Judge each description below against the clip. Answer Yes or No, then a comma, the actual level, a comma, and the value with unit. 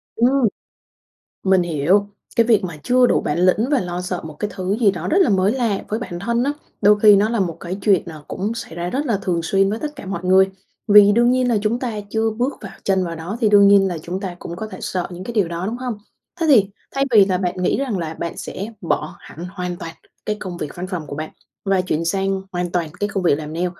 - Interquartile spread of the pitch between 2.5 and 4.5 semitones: Yes, average, 3.9 semitones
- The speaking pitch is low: No, high, 195 Hz